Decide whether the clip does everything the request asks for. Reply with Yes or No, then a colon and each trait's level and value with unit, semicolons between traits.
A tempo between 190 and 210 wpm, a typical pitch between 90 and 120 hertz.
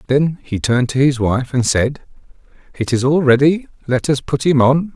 No: fast, 205 wpm; low, 135 Hz